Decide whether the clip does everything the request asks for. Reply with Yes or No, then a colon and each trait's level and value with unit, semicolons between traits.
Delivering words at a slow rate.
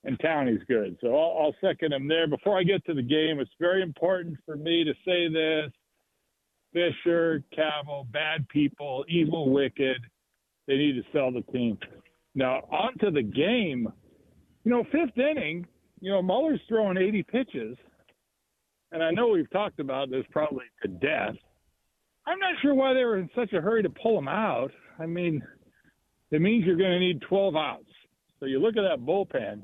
No: average, 180 wpm